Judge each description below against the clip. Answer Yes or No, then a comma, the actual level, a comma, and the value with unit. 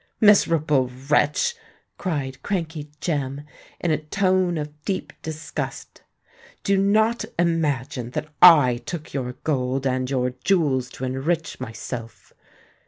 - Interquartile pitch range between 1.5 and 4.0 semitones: No, average, 4.7 semitones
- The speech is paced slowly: Yes, slow, 115 wpm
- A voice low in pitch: No, medium, 150 Hz